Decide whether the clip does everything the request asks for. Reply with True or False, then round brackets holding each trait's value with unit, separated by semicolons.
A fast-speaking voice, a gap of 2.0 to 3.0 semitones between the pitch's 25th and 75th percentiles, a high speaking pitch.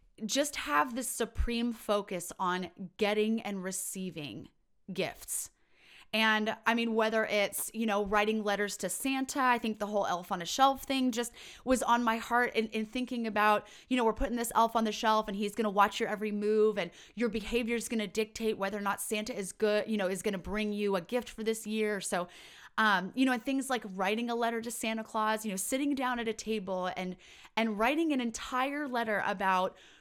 True (210 wpm; 2.7 semitones; 220 Hz)